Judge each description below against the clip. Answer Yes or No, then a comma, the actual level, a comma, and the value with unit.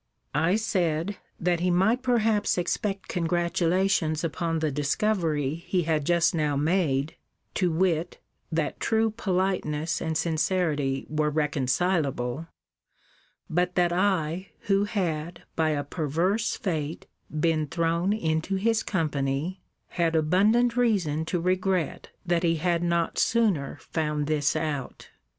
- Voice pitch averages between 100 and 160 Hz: No, medium, 170 Hz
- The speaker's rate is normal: No, slow, 125 wpm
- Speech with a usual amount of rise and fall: Yes, average, 3.5 semitones